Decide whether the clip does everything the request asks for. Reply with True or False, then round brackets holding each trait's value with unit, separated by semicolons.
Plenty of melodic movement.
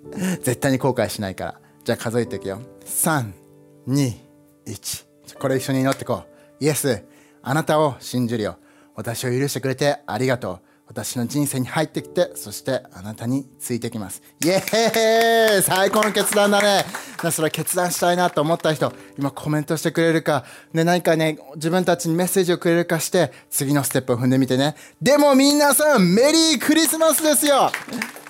True (6.0 semitones)